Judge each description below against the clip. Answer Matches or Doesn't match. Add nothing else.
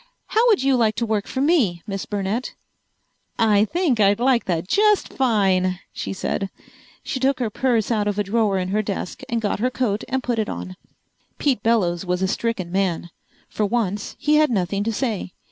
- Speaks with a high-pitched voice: Matches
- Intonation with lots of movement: Doesn't match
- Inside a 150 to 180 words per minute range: Doesn't match